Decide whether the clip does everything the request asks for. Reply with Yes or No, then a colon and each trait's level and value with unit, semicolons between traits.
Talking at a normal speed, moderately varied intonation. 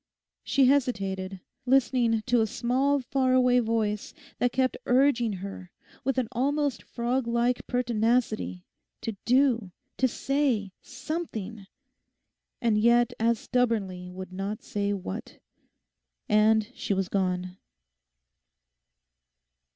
No: slow, 110 wpm; average, 3.8 semitones